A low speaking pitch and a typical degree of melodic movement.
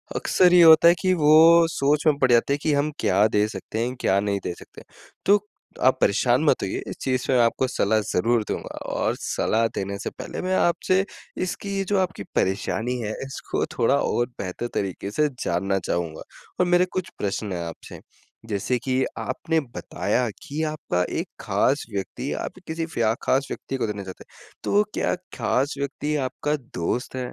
No: low, 130 Hz; wide, 7.0 semitones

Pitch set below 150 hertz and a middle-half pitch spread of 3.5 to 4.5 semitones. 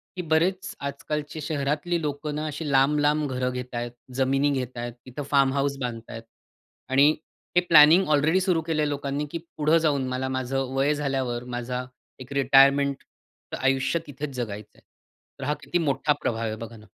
No: medium, 140 Hz; average, 2.8 semitones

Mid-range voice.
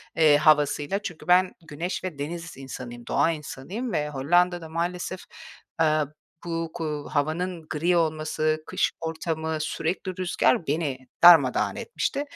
Yes: medium, 160 Hz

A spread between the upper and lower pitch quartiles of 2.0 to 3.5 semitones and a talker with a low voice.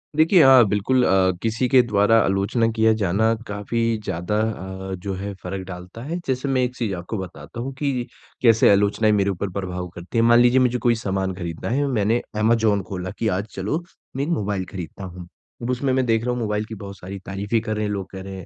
No: average, 3.9 semitones; low, 105 Hz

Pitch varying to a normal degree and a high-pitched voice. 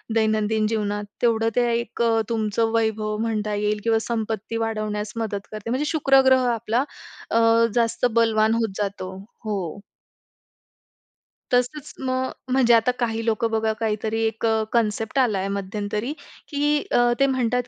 No: narrow, 1.7 semitones; high, 225 Hz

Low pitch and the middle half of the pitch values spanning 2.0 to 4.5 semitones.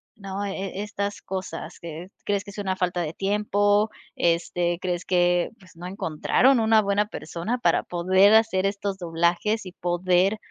No: high, 190 Hz; narrow, 2.6 semitones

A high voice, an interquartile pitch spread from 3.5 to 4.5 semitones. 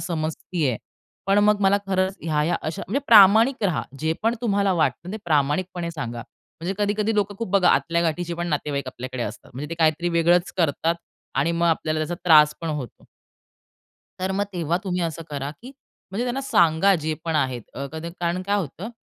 No: medium, 170 Hz; average, 4.0 semitones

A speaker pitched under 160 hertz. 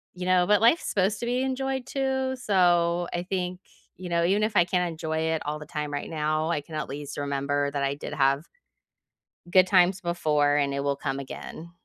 No: medium, 170 Hz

